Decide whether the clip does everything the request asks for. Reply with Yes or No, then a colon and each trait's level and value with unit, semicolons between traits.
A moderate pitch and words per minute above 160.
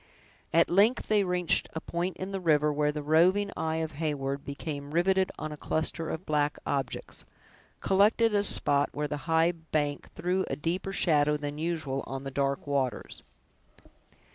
Yes: medium, 160 Hz; average, 170 wpm